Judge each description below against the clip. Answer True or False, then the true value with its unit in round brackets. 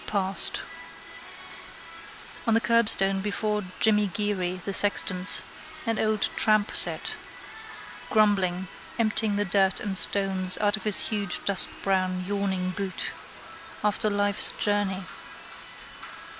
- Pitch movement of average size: False (1.8 semitones)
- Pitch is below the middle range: False (200 Hz)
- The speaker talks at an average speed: False (105 wpm)